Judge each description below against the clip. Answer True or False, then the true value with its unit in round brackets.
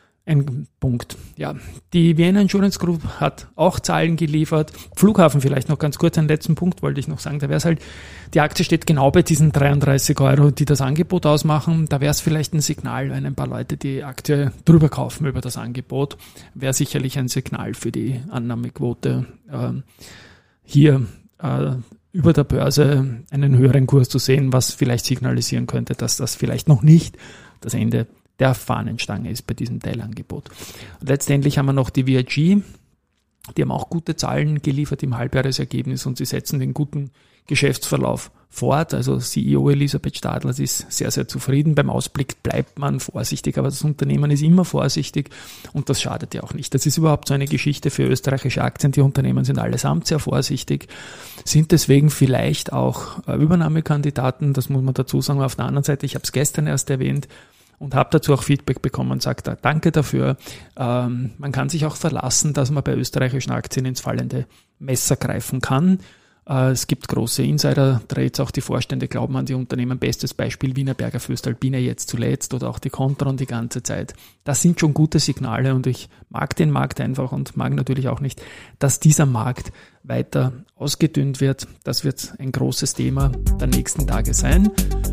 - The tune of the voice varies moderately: True (3.0 semitones)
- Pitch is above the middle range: False (135 Hz)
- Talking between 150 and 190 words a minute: True (180 wpm)